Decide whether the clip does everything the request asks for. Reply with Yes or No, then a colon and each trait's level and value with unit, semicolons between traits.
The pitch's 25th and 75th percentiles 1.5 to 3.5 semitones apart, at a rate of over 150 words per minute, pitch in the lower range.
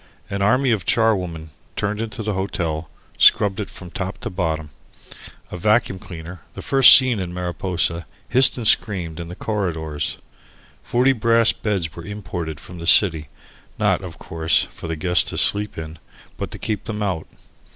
No: average, 4.4 semitones; average, 170 wpm; very low, 90 Hz